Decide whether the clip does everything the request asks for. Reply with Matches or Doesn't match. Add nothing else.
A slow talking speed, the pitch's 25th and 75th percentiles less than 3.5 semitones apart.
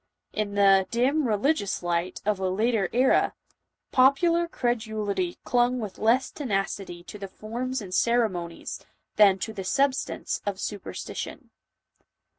Doesn't match